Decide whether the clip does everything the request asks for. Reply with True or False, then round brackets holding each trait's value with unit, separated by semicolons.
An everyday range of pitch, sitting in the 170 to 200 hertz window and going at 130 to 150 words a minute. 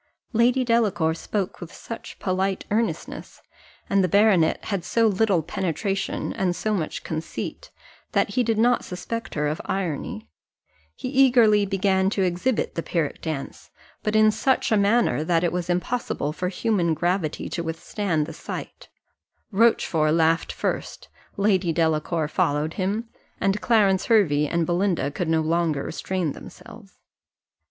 True (4.6 semitones; 185 Hz; 145 wpm)